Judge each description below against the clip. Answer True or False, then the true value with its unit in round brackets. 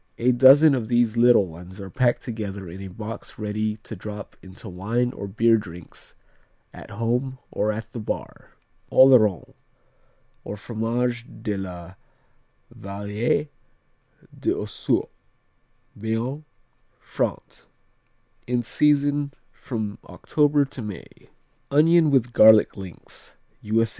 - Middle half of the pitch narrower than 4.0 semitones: True (3.4 semitones)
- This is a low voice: True (115 Hz)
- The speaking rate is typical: False (115 wpm)